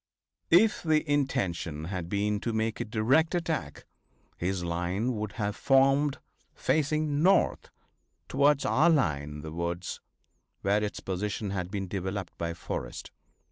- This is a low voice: Yes, low, 105 Hz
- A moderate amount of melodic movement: No, wide, 8.1 semitones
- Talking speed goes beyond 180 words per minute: No, average, 140 wpm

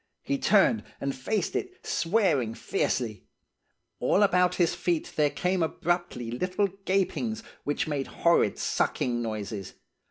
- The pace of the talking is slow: Yes, slow, 125 wpm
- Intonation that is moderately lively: No, wide, 7.3 semitones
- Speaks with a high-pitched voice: No, medium, 170 Hz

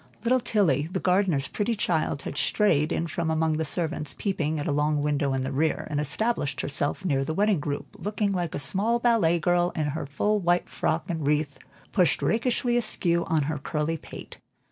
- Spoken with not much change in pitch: No, average, 5.0 semitones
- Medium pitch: Yes, medium, 160 Hz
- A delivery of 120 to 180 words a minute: No, average, 195 wpm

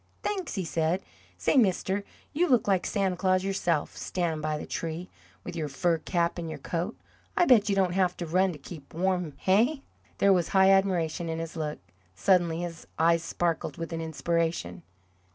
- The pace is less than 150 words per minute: No, average, 185 wpm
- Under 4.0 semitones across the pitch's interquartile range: Yes, average, 2.8 semitones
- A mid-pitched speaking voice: Yes, medium, 175 Hz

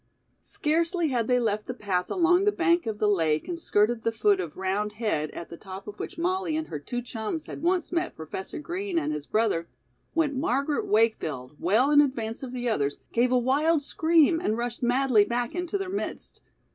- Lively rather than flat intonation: Yes, wide, 7.7 semitones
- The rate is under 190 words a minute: No, fast, 205 wpm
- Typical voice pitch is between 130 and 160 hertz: No, high, 245 Hz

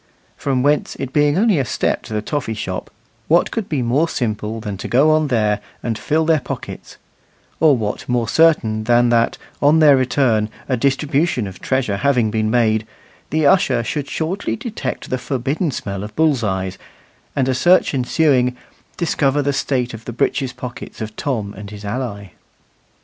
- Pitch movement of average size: Yes, average, 5.0 semitones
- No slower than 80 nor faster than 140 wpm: No, average, 175 wpm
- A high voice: No, low, 125 Hz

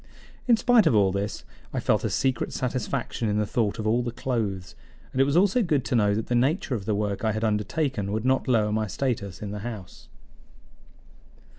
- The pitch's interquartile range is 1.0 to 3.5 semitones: No, average, 4.2 semitones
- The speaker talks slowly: No, fast, 205 wpm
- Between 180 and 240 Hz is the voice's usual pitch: No, low, 110 Hz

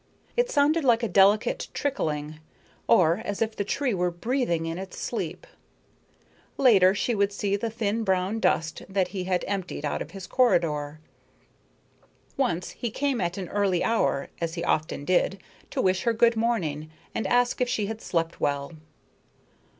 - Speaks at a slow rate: No, average, 165 wpm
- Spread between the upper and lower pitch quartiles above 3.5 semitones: Yes, average, 5.2 semitones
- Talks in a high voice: Yes, high, 195 Hz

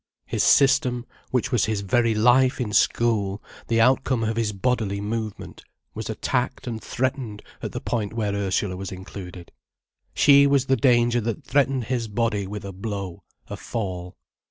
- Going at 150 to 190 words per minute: Yes, average, 160 wpm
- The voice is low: Yes, low, 115 Hz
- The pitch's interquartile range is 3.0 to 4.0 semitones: Yes, average, 3.7 semitones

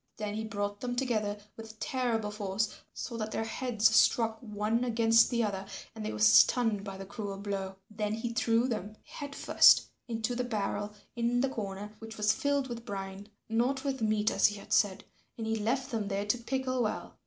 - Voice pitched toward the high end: Yes, high, 220 Hz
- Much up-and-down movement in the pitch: No, narrow, 2.5 semitones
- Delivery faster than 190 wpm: Yes, average, 200 wpm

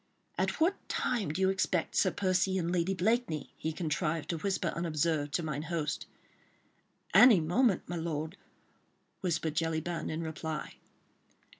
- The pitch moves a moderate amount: Yes, average, 3.0 semitones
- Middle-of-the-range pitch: Yes, medium, 170 Hz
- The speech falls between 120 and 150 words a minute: Yes, average, 140 wpm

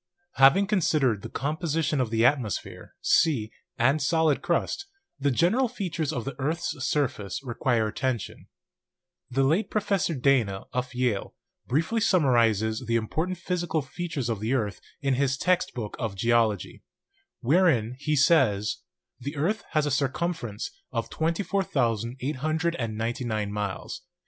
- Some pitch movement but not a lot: No, wide, 5.9 semitones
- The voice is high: No, low, 135 Hz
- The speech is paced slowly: Yes, slow, 130 wpm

